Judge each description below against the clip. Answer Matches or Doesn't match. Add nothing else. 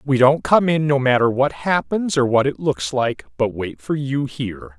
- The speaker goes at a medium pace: Doesn't match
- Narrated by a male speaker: Matches